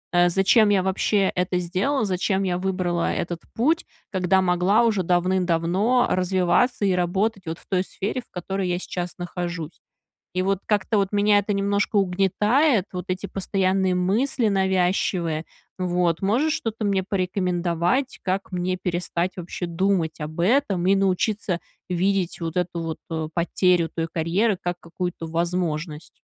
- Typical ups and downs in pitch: No, narrow, 2.2 semitones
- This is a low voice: No, medium, 185 Hz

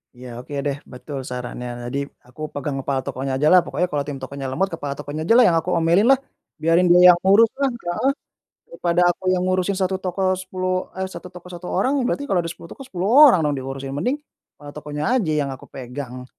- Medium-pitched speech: Yes, medium, 170 Hz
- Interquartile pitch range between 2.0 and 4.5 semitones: No, average, 5.1 semitones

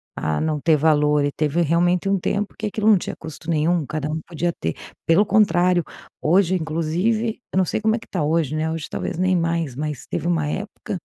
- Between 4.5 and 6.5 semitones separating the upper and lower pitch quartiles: No, average, 3.4 semitones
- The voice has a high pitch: No, medium, 165 Hz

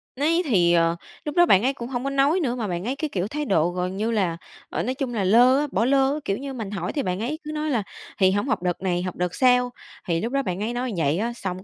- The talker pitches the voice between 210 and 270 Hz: Yes, high, 230 Hz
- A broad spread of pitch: Yes, wide, 6.8 semitones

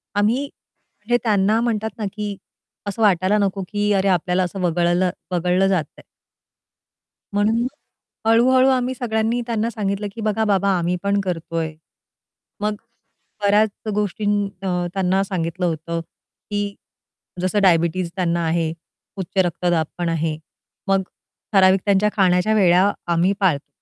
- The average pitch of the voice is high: Yes, high, 195 Hz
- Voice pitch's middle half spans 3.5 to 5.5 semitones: No, average, 3.1 semitones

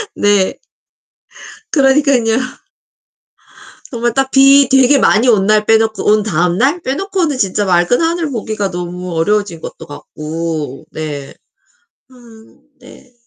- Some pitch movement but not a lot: No, wide, 7.1 semitones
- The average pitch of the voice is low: No, high, 215 Hz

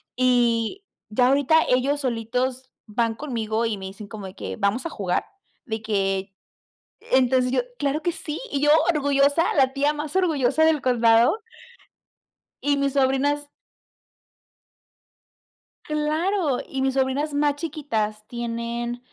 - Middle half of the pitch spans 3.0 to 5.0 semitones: Yes, average, 4.0 semitones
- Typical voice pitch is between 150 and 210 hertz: No, very high, 260 Hz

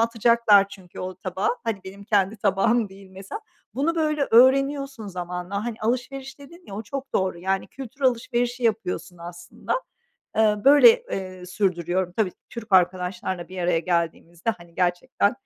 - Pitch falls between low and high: No, high, 200 Hz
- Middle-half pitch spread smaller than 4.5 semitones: No, average, 4.9 semitones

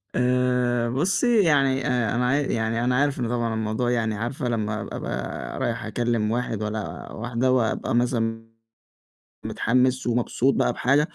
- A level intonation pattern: Yes, narrow, 2.1 semitones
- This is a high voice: No, low, 120 Hz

